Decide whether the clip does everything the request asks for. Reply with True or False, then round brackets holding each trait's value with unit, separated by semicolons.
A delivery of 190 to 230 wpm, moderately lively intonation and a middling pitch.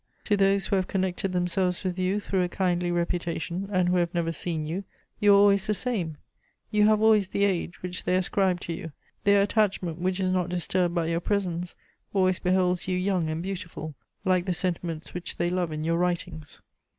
False (200 wpm; 2.0 semitones; 180 Hz)